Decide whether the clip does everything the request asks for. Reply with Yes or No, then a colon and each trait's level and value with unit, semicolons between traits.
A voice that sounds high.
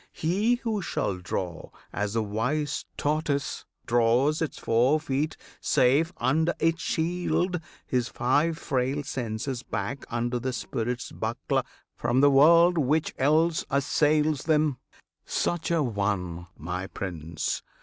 No: low, 135 Hz